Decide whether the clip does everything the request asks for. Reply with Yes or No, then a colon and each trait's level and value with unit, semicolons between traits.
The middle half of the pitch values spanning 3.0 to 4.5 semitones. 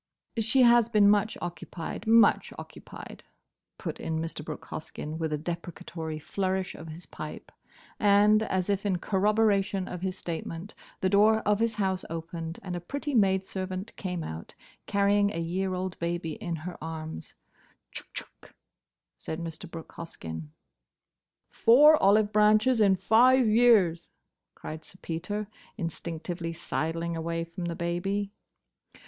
Yes: average, 3.9 semitones